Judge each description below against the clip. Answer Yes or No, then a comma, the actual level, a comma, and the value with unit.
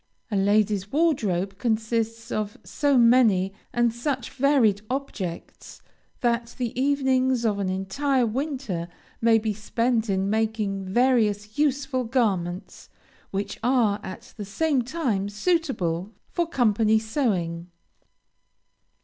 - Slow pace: Yes, slow, 115 wpm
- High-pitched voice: Yes, high, 225 Hz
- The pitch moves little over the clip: No, average, 4.4 semitones